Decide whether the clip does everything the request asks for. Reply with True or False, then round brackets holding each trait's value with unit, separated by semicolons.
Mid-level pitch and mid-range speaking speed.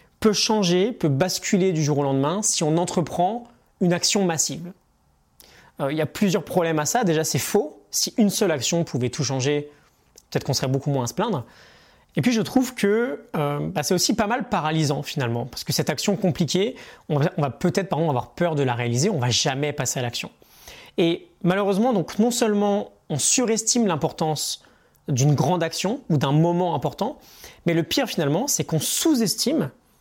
True (165 Hz; 195 wpm)